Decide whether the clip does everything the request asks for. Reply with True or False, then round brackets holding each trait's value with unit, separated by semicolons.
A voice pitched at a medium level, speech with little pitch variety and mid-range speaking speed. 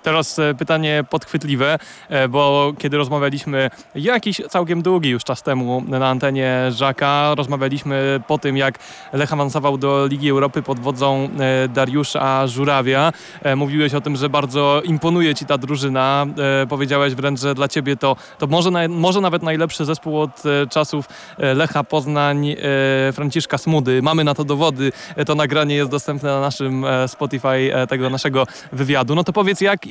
True (145 Hz; 2.1 semitones; 150 wpm)